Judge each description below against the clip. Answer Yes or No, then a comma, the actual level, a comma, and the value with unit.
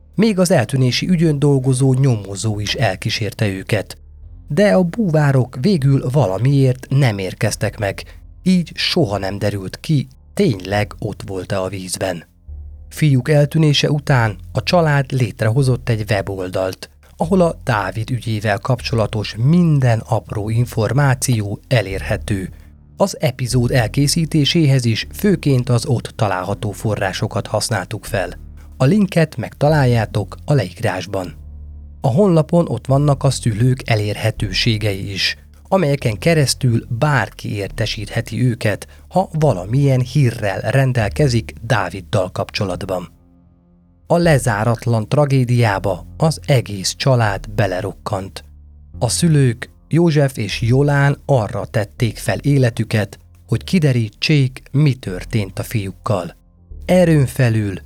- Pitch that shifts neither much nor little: No, wide, 6.2 semitones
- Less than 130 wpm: Yes, average, 110 wpm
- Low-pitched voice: Yes, low, 115 Hz